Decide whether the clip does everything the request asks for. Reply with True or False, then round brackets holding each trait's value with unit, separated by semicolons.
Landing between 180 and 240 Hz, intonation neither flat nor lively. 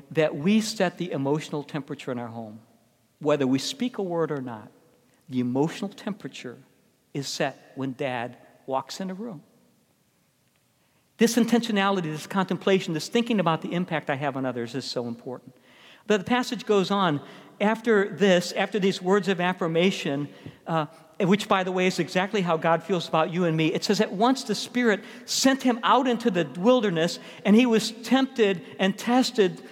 False (185 Hz; 6.3 semitones)